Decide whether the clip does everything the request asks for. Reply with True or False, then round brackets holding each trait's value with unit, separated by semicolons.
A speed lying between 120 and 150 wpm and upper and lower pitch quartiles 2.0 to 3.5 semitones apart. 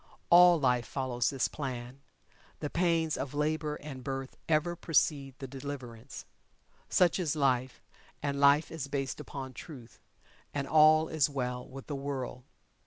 True (145 wpm; 2.9 semitones)